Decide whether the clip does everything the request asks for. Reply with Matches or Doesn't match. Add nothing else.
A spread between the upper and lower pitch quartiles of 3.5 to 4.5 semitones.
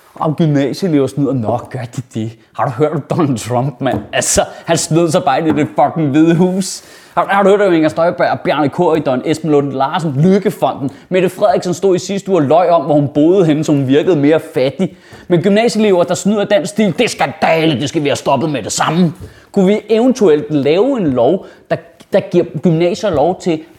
Matches